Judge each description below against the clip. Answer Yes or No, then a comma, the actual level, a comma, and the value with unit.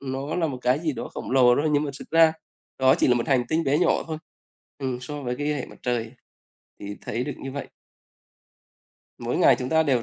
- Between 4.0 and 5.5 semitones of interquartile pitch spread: No, average, 3.0 semitones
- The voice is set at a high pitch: No, low, 135 Hz